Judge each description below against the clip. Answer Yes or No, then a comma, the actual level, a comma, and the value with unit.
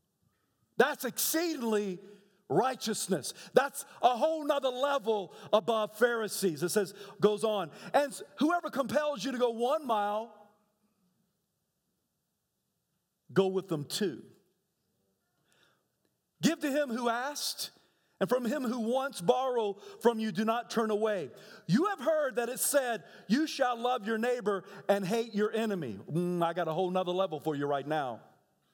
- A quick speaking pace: No, average, 145 wpm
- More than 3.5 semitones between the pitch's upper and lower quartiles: Yes, average, 4.7 semitones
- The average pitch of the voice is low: No, high, 225 Hz